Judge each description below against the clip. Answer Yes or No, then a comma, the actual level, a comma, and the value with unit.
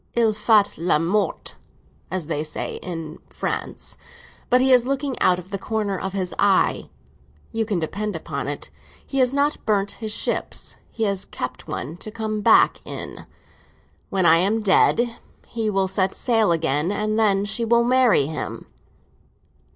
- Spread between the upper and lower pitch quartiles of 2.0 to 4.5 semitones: Yes, average, 4.0 semitones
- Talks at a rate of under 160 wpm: No, average, 165 wpm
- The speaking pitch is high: Yes, high, 205 Hz